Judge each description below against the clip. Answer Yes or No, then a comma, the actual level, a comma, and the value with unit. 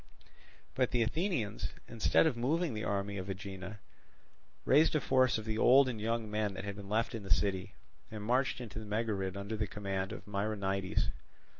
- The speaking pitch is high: No, low, 105 Hz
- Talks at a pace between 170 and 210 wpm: Yes, average, 185 wpm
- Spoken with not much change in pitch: No, average, 3.1 semitones